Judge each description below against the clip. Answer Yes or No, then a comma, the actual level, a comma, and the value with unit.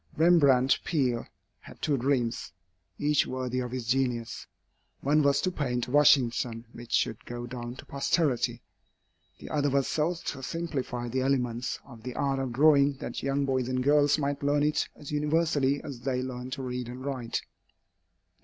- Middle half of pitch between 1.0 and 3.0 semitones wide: Yes, average, 2.7 semitones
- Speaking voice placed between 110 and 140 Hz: Yes, low, 135 Hz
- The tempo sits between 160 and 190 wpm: Yes, average, 170 wpm